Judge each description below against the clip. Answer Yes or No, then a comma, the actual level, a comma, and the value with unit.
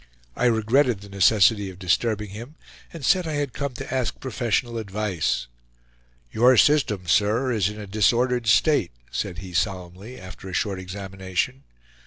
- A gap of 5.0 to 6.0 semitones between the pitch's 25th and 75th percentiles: No, average, 4.6 semitones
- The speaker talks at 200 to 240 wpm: No, average, 155 wpm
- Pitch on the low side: Yes, low, 110 Hz